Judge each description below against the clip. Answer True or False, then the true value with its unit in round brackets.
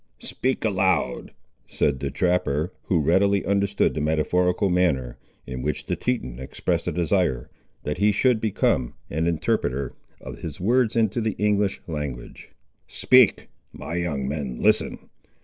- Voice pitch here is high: False (90 Hz)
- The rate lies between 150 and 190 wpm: False (140 wpm)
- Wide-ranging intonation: True (5.9 semitones)